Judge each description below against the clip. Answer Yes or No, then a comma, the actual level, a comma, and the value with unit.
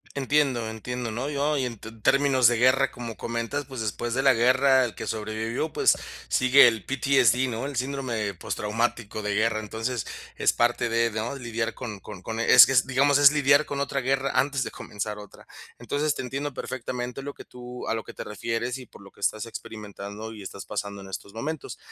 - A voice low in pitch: Yes, low, 120 Hz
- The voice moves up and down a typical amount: Yes, average, 3.4 semitones